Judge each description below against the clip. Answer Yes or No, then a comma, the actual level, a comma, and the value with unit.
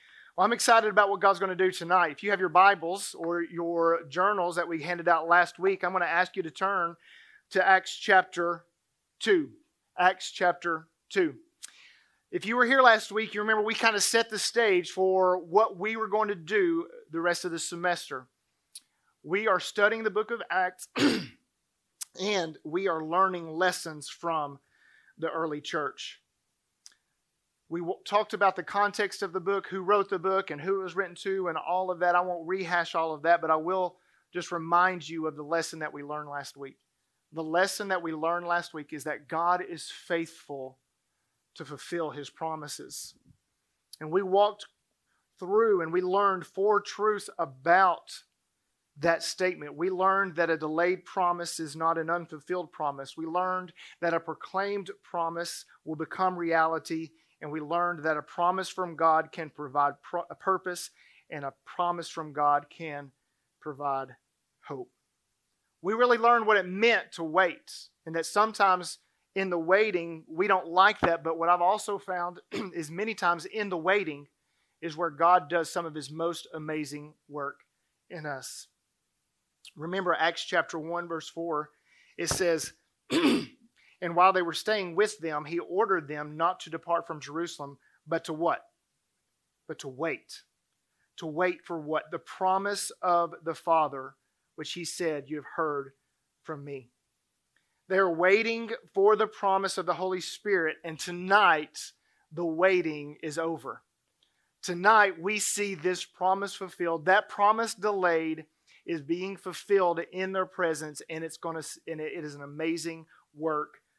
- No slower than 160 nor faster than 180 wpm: Yes, average, 165 wpm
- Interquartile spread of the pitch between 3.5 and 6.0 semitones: No, average, 3.1 semitones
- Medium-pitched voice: Yes, medium, 175 Hz